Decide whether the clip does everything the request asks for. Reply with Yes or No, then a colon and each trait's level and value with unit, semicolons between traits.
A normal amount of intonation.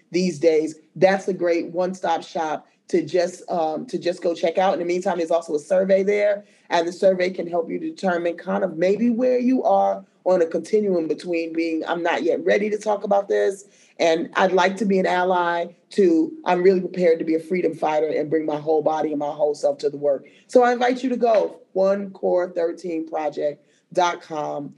Yes: average, 3.1 semitones